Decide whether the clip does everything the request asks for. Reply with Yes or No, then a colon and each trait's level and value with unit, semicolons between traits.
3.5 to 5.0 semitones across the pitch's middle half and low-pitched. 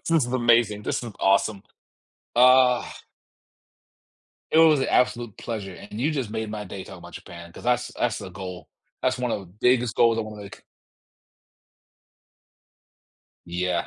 Yes: average, 3.9 semitones; low, 115 Hz